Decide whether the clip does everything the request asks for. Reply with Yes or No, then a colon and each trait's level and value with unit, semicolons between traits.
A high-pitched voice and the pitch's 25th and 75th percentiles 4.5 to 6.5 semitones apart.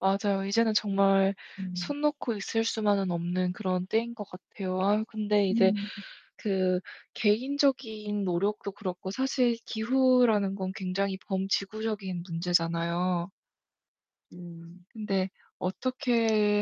No: high, 200 Hz; average, 3.1 semitones